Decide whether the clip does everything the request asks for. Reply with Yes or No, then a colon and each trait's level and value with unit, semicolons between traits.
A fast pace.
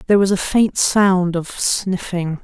No: average, 175 wpm